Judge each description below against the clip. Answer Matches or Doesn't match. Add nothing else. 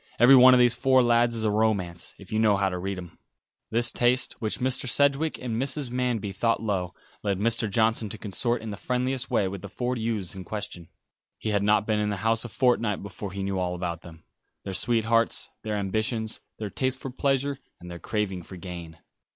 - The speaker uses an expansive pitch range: Doesn't match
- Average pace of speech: Doesn't match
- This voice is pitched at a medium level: Doesn't match